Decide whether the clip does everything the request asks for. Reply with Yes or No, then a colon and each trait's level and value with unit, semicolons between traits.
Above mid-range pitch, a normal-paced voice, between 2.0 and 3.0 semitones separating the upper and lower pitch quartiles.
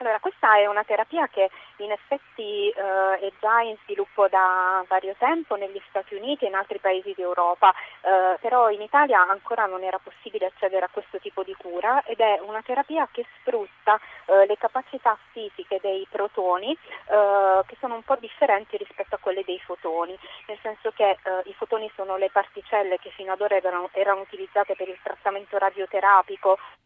No: high, 200 Hz; fast, 180 wpm; narrow, 2.6 semitones